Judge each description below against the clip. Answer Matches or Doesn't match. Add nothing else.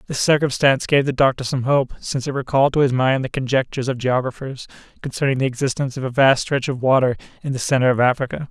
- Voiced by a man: Matches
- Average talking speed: Doesn't match